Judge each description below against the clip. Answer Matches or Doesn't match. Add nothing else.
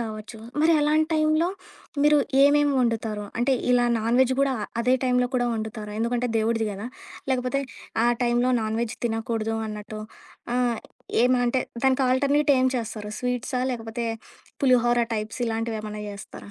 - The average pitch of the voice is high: Matches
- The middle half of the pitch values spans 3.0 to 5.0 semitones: Doesn't match